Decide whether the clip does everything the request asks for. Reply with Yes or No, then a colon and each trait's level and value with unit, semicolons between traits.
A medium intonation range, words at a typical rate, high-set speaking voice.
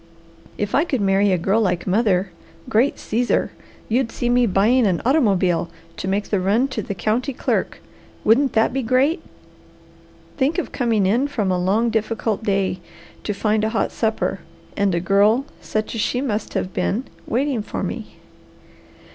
Yes: average, 3.9 semitones; average, 170 wpm; high, 220 Hz